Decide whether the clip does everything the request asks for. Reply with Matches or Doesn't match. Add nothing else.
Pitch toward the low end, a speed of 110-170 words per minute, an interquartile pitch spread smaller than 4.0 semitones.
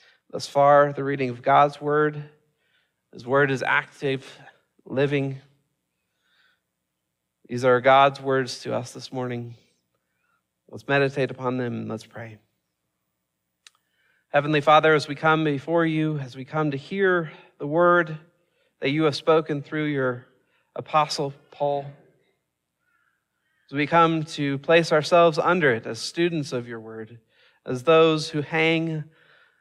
Doesn't match